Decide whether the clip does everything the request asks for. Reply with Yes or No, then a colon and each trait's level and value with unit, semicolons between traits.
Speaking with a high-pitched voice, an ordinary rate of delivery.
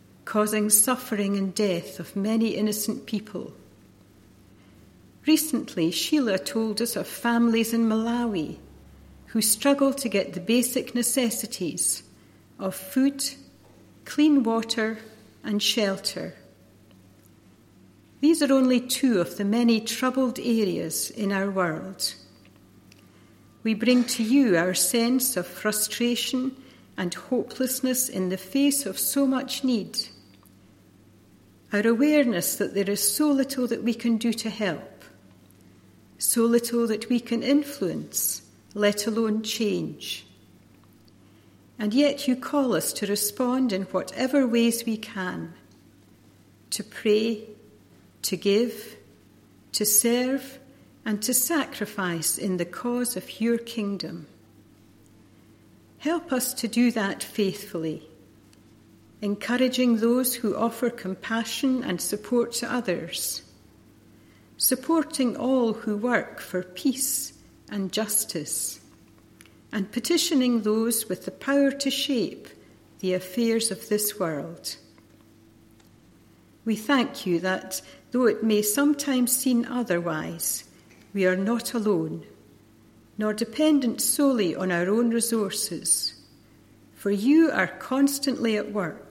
No: high, 210 Hz; slow, 115 wpm